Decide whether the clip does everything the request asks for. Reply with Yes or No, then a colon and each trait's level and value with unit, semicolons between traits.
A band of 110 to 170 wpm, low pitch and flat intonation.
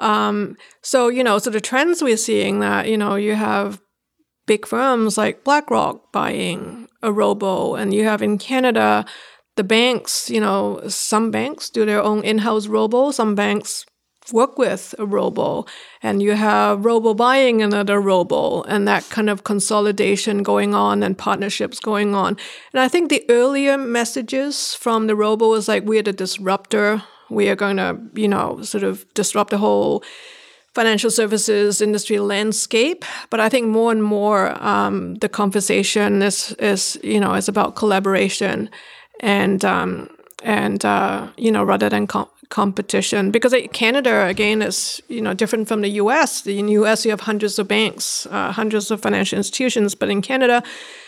No: average, 165 wpm; high, 215 Hz; narrow, 2.3 semitones